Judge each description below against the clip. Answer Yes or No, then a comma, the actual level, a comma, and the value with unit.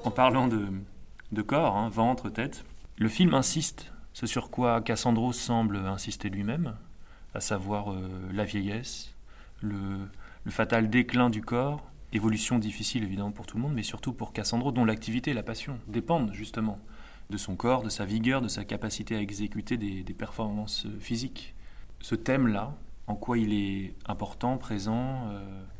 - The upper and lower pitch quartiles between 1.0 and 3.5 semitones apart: Yes, average, 3.0 semitones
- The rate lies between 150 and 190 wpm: Yes, average, 165 wpm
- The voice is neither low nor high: No, low, 110 Hz